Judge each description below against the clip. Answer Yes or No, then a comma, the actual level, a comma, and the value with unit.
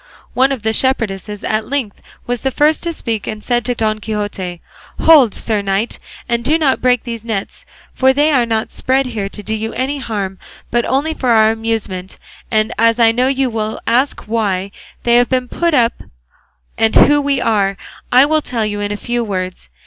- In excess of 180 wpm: Yes, average, 200 wpm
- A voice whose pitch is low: No, high, 230 Hz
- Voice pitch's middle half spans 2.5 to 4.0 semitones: Yes, average, 3.5 semitones